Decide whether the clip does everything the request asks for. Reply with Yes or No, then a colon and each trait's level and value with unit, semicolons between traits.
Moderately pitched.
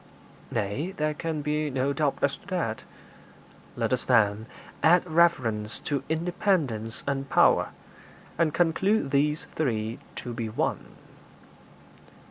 Yes: medium, 145 Hz